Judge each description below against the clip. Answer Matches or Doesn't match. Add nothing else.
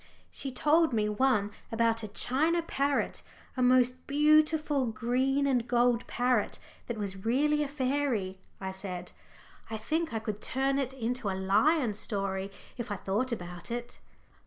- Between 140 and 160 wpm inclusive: Matches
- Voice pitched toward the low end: Doesn't match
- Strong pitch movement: Doesn't match